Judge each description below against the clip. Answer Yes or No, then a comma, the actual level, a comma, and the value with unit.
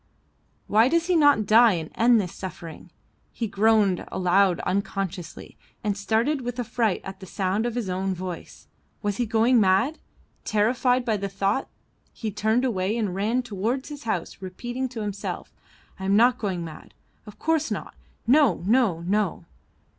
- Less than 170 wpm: Yes, average, 160 wpm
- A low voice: No, high, 210 Hz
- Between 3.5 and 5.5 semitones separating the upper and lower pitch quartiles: Yes, average, 4.1 semitones